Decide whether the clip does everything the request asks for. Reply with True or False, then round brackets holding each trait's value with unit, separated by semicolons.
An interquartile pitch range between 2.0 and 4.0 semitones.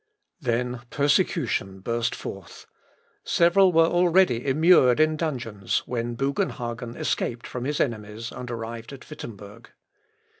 False (5.0 semitones)